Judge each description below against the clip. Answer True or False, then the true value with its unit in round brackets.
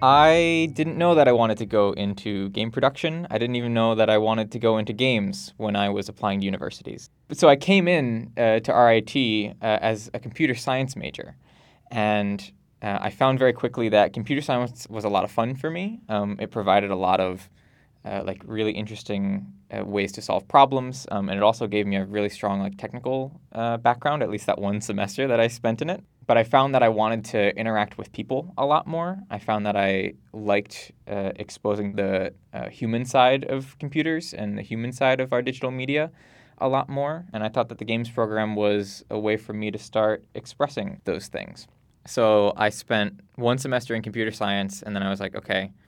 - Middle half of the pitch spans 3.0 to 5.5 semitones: True (3.9 semitones)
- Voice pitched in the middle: False (110 Hz)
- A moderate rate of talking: False (215 wpm)